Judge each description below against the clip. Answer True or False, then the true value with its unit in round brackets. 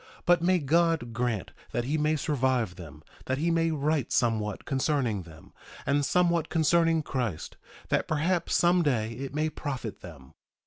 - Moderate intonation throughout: False (6.1 semitones)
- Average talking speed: True (160 wpm)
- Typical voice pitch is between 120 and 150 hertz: True (140 Hz)